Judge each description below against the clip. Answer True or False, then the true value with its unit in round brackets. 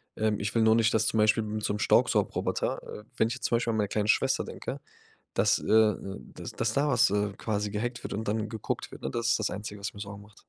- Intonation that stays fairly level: True (1.5 semitones)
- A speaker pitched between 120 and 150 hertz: False (110 Hz)